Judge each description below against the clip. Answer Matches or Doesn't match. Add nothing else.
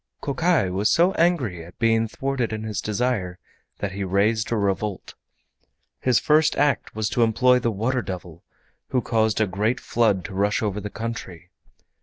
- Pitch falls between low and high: Doesn't match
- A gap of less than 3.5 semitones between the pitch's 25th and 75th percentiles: Doesn't match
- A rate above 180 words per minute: Doesn't match